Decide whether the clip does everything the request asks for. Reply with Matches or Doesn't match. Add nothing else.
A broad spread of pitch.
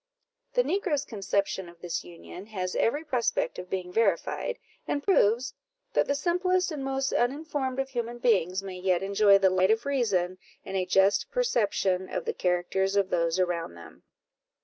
Matches